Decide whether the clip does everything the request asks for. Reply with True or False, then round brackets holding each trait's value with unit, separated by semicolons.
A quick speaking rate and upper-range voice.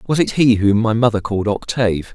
False (225 wpm; 110 Hz)